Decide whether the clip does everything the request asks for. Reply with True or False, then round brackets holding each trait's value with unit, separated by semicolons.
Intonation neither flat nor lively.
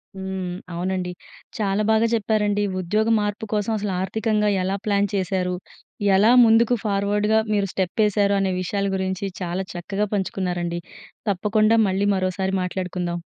False (2.2 semitones)